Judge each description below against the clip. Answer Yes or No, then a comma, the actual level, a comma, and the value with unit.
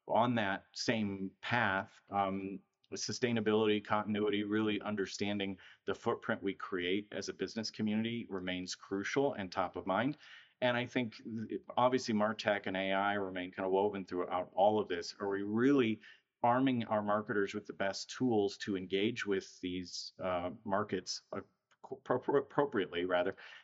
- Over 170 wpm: No, average, 145 wpm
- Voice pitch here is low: Yes, low, 100 Hz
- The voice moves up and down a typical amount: No, narrow, 2.3 semitones